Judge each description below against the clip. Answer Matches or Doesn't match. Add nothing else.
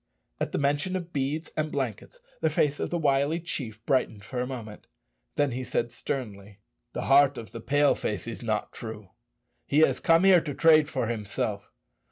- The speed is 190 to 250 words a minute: Matches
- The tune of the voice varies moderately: Matches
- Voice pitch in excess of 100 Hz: Matches